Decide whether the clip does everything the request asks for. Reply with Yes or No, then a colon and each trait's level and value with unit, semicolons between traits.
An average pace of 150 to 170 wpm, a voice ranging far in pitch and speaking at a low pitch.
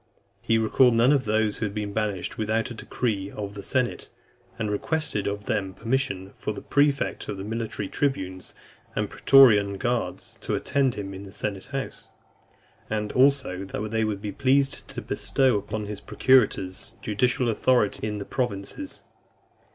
No: average, 165 wpm; average, 4.1 semitones; low, 110 Hz